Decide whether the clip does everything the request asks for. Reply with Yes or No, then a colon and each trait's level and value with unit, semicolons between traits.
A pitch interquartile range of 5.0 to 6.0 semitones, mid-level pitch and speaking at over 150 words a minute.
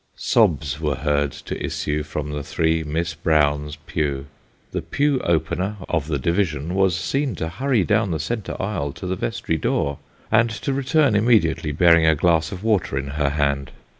No: wide, 5.5 semitones; very low, 80 Hz; average, 175 wpm